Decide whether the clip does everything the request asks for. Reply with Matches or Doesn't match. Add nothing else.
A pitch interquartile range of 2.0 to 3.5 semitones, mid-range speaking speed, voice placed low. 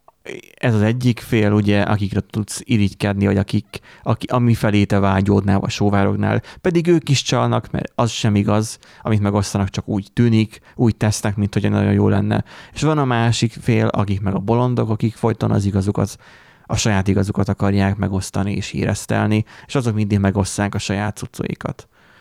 Doesn't match